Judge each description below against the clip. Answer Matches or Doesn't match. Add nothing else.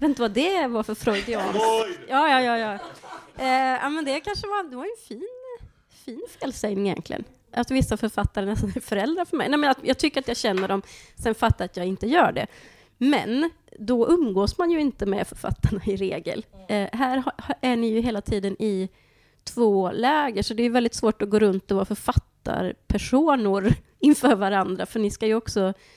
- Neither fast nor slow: Doesn't match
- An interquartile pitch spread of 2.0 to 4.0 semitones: Doesn't match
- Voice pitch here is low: Doesn't match